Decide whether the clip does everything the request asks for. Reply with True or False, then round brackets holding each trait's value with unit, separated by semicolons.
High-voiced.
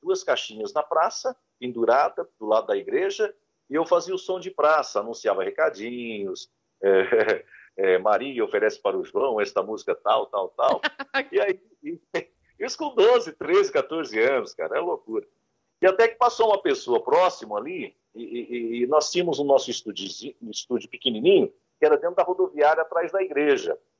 True (355 Hz)